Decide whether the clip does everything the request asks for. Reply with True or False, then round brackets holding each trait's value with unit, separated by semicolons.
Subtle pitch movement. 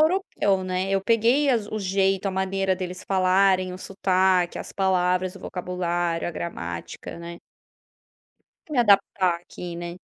True (1.6 semitones)